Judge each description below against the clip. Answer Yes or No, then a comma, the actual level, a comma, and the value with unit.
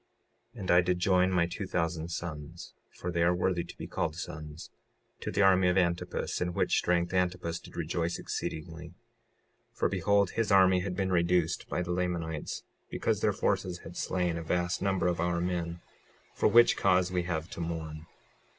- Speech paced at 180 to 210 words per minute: Yes, average, 185 wpm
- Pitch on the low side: Yes, very low, 90 Hz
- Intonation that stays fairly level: Yes, narrow, 1.4 semitones